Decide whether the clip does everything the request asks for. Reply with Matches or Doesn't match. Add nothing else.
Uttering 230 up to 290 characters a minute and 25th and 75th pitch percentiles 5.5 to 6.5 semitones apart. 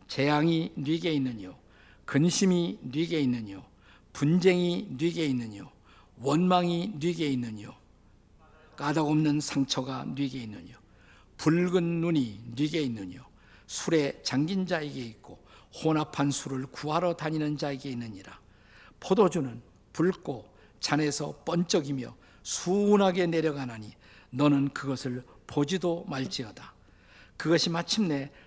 Matches